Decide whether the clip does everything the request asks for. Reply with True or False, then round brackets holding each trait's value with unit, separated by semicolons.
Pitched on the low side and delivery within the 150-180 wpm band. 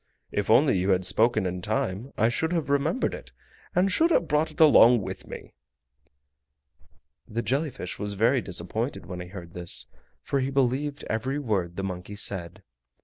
True (115 Hz; 175 wpm)